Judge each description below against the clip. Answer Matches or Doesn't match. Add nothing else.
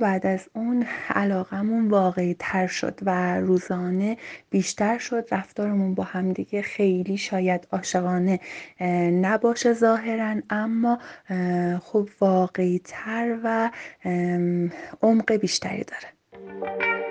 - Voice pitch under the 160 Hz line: Doesn't match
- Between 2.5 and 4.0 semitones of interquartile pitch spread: Matches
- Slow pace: Matches